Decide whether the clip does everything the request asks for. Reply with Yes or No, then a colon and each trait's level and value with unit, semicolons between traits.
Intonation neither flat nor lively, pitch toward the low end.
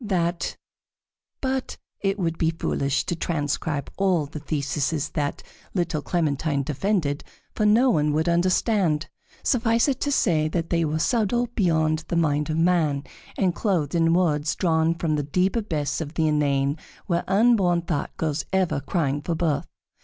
No: average, 3.8 semitones; medium, 165 Hz